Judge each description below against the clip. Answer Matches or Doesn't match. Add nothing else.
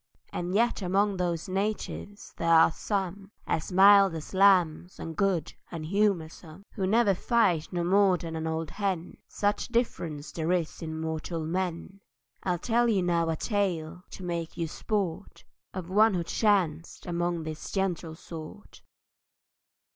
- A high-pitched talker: Doesn't match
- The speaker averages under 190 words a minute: Matches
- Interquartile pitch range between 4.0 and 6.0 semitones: Doesn't match